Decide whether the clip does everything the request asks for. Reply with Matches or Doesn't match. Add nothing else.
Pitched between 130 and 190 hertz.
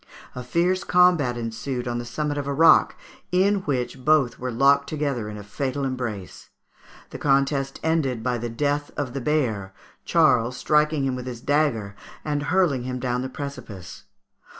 Matches